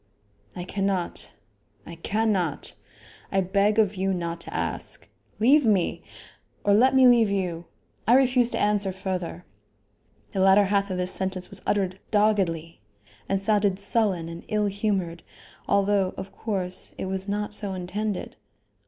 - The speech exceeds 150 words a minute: No, average, 145 wpm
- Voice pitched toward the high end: Yes, high, 195 Hz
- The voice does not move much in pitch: Yes, narrow, 2.3 semitones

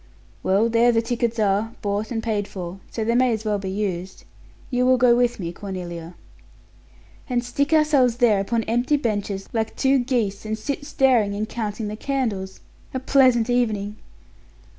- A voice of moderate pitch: No, high, 225 Hz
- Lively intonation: No, average, 3.4 semitones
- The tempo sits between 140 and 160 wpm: No, average, 170 wpm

